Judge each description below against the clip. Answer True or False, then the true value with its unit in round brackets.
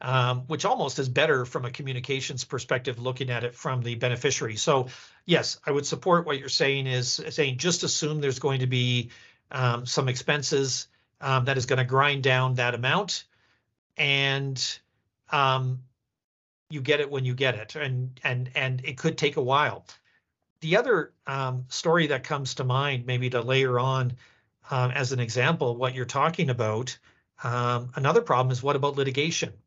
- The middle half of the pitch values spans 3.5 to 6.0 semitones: False (2.5 semitones)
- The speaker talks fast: False (175 wpm)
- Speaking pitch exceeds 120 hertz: True (130 Hz)